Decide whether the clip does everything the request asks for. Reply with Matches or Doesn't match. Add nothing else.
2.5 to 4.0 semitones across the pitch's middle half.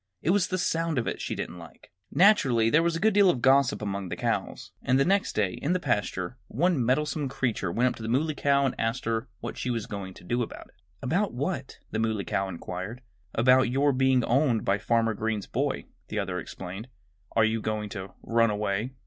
Doesn't match